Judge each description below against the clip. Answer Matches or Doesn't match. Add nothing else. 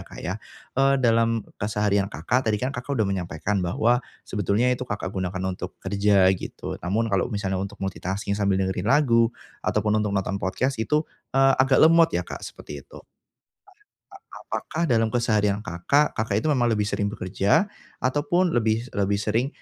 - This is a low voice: Matches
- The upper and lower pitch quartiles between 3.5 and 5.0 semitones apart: Matches